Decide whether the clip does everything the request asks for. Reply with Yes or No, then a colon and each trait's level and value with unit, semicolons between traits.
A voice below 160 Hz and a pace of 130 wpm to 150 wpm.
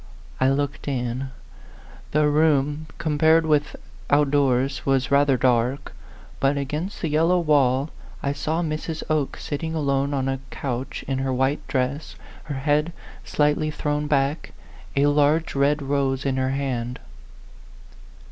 Yes: medium, 140 Hz; average, 140 wpm